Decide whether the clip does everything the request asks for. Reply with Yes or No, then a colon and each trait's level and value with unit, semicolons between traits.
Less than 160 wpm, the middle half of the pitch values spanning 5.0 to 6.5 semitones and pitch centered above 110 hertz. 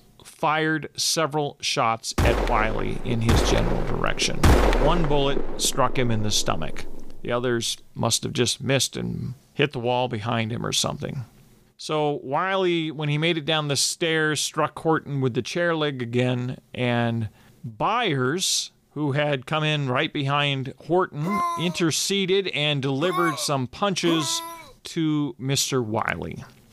No: average, 140 wpm; average, 4.4 semitones; medium, 140 Hz